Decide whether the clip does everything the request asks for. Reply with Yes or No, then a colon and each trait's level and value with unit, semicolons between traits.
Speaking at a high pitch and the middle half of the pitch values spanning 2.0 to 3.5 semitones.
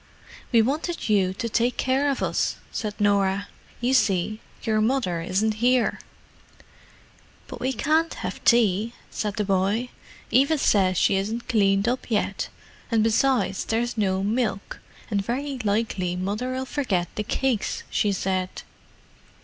No: high, 215 Hz; average, 4.2 semitones